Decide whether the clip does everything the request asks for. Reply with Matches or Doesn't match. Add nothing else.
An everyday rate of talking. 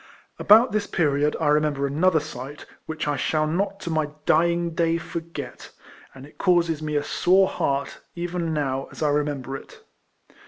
Matches